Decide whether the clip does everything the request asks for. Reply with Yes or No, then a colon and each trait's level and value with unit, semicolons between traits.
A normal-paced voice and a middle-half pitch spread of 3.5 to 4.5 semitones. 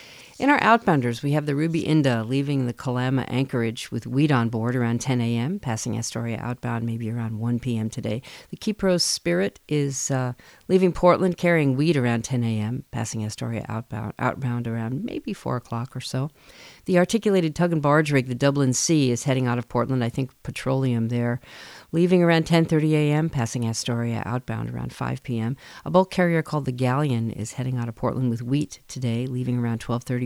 Yes: average, 185 wpm; average, 4.2 semitones